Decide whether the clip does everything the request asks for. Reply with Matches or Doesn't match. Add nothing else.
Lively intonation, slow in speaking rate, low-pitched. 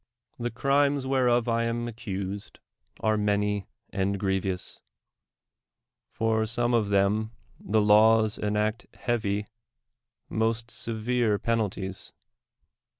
Doesn't match